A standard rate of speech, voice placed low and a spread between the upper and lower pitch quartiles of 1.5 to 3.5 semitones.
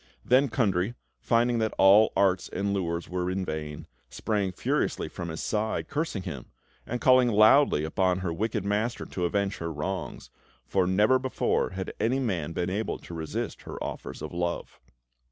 No: average, 170 wpm; very low, 95 Hz; average, 4.2 semitones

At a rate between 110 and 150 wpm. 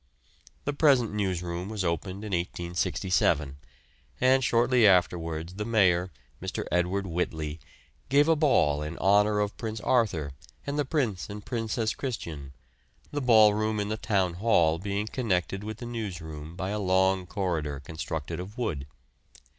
Yes: average, 145 wpm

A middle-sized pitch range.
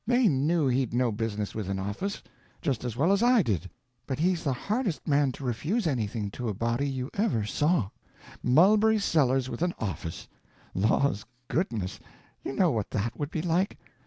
No: wide, 7.8 semitones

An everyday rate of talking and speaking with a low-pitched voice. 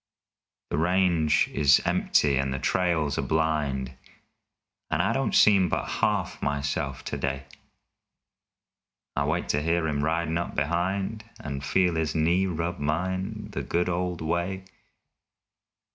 No: slow, 130 wpm; very low, 80 Hz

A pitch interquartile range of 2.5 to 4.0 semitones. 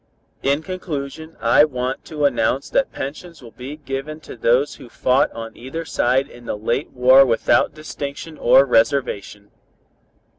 Yes: average, 3.4 semitones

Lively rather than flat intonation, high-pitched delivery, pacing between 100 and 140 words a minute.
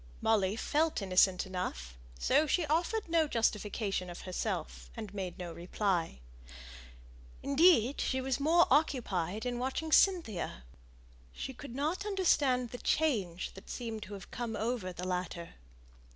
Yes: wide, 7.6 semitones; high, 225 Hz; slow, 135 wpm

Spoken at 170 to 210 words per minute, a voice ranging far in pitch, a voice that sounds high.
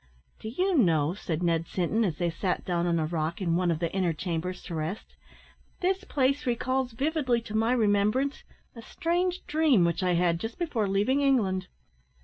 Yes: average, 185 wpm; wide, 7.2 semitones; high, 200 Hz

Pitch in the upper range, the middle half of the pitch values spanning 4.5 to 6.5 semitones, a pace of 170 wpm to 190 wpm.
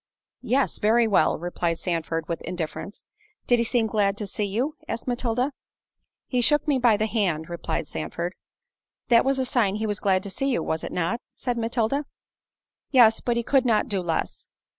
Yes: high, 220 Hz; average, 5.0 semitones; average, 185 wpm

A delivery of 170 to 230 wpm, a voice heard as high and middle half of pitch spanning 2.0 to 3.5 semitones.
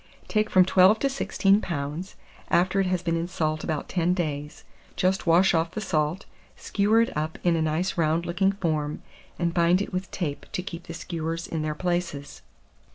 No: average, 190 wpm; medium, 175 Hz; average, 2.8 semitones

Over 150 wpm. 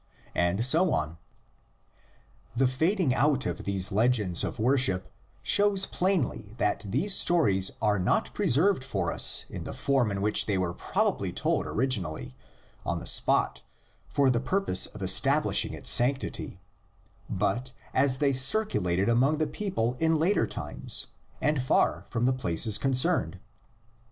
No: average, 145 wpm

